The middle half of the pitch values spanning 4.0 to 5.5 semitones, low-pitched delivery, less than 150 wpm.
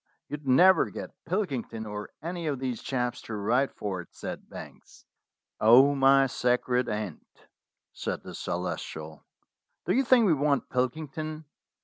Yes: average, 5.2 semitones; low, 130 Hz; average, 140 wpm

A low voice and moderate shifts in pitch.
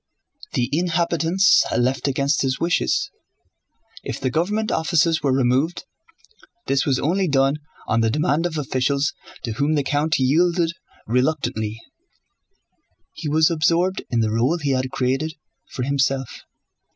No: medium, 145 Hz; average, 4.2 semitones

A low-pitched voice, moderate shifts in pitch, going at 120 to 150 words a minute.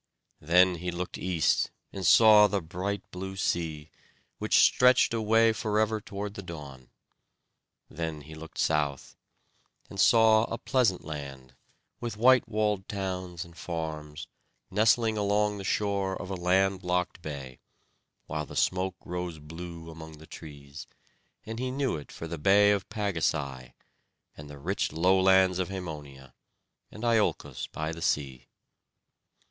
Yes: very low, 90 Hz; average, 4.7 semitones; average, 140 wpm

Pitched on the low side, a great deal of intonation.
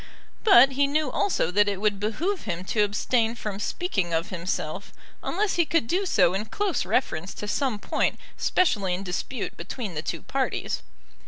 No: high, 215 Hz; wide, 7.4 semitones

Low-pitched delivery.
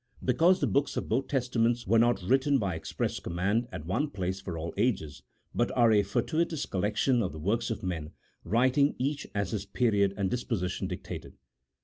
Yes: low, 110 Hz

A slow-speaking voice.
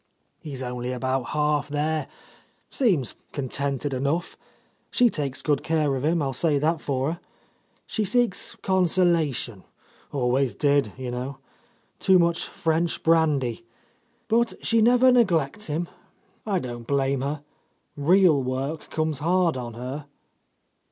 Yes: slow, 130 wpm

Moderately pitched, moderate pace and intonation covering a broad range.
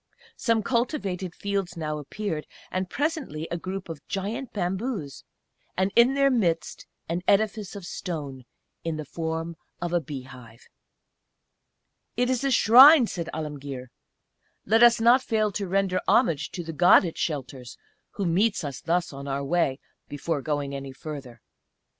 Yes: medium, 175 Hz; average, 155 wpm; wide, 6.3 semitones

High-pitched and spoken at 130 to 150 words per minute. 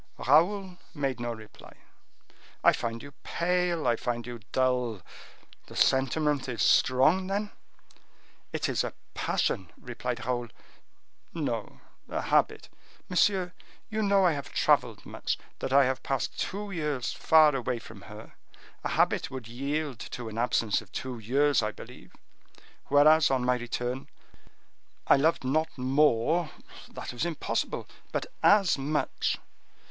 No: low, 135 Hz; slow, 135 wpm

